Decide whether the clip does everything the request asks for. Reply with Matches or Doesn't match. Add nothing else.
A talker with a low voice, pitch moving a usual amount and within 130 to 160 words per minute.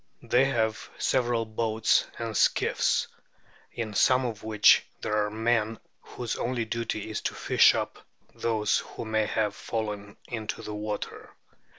Doesn't match